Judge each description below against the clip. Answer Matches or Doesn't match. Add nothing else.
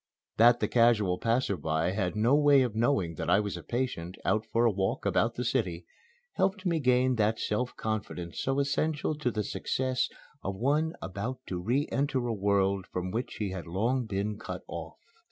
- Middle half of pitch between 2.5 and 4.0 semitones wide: Doesn't match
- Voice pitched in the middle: Doesn't match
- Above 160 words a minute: Matches